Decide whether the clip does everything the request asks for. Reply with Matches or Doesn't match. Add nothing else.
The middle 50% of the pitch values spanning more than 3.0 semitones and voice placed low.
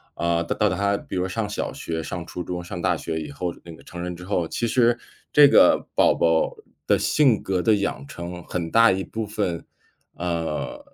Matches